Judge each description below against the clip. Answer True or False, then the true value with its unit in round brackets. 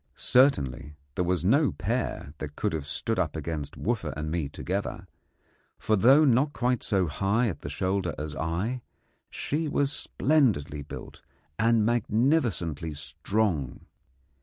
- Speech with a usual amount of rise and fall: False (7.9 semitones)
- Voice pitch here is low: True (95 Hz)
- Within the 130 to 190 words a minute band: True (135 wpm)